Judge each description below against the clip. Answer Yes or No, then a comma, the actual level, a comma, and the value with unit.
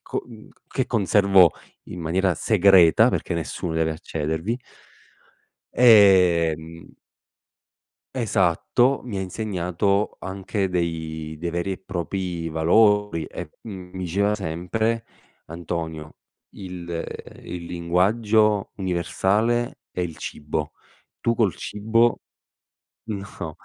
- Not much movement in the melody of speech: No, average, 3.7 semitones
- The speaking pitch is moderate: No, very low, 90 Hz